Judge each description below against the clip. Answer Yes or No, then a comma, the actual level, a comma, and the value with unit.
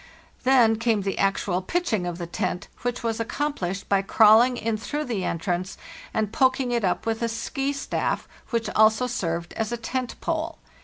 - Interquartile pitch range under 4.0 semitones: No, average, 4.3 semitones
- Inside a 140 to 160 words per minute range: No, average, 170 wpm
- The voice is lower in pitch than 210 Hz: No, high, 225 Hz